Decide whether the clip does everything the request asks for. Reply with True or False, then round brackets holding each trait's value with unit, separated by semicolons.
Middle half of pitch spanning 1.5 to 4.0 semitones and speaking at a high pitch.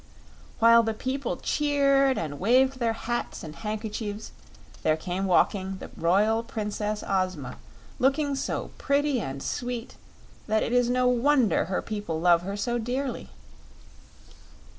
False (4.7 semitones; 225 Hz)